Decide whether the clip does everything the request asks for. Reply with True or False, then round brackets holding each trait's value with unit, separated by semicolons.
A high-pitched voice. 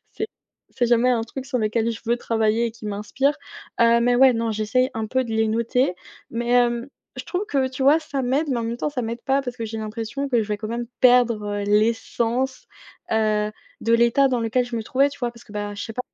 True (235 Hz)